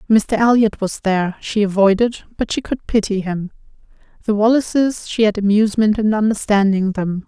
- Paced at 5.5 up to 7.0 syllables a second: No, 5.2 syllables/s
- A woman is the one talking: Yes, female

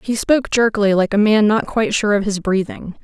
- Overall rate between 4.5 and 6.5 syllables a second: Yes, 5.9 syllables/s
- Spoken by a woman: Yes, female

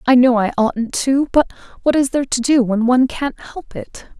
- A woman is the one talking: Yes, female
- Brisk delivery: Yes, fast, 230 wpm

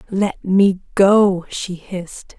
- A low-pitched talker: No, high, 190 Hz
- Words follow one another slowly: Yes, slow, 125 wpm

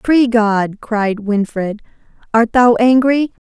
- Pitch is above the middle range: Yes, high, 225 Hz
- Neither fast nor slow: No, slow, 120 wpm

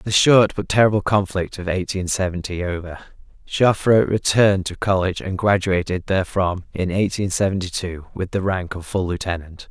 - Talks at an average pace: Yes, average, 160 wpm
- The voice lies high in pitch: No, very low, 95 Hz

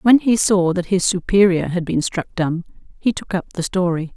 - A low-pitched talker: No, medium, 185 Hz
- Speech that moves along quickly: Yes, fast, 215 wpm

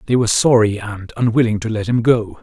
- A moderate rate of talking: No, fast, 225 wpm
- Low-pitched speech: Yes, low, 110 Hz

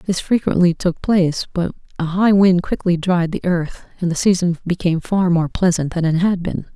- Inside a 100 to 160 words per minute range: No, fast, 205 wpm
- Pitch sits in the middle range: Yes, medium, 175 Hz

